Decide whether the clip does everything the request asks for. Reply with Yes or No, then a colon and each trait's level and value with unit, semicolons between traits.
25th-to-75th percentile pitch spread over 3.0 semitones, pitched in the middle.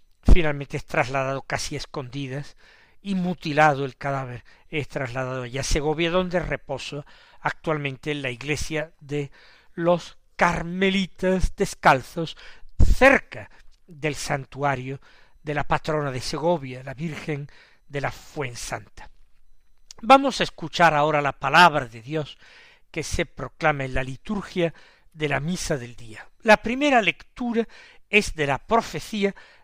Yes: average, 4.3 semitones; medium, 150 Hz